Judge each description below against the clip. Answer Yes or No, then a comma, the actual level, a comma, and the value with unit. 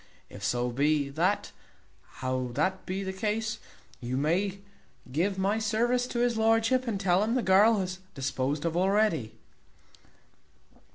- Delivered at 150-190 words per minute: No, average, 140 wpm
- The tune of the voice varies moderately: No, wide, 6.9 semitones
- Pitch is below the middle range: No, high, 190 Hz